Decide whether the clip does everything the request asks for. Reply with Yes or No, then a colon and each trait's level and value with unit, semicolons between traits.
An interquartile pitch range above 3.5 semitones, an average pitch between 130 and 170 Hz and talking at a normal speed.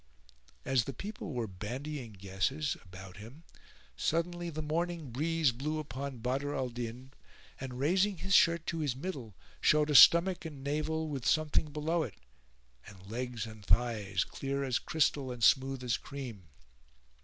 Yes: average, 4.7 semitones; low, 135 Hz; average, 155 wpm